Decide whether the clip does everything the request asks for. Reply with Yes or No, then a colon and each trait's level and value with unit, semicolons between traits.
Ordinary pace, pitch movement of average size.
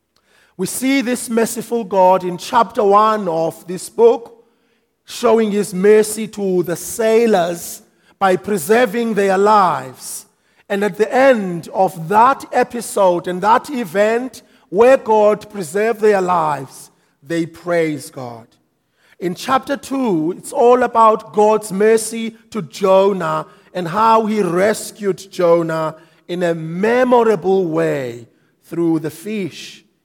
No: slow, 120 wpm; average, 4.5 semitones